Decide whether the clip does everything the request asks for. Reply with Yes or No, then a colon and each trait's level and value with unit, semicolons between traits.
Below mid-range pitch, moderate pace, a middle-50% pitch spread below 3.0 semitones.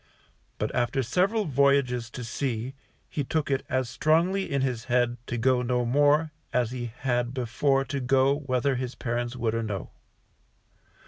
Yes: low, 130 Hz; average, 160 wpm; narrow, 2.6 semitones